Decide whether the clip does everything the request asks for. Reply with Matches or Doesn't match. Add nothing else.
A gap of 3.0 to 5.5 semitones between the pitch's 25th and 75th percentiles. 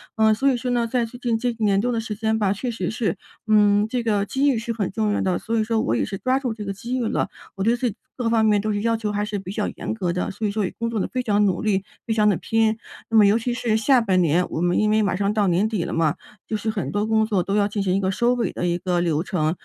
Doesn't match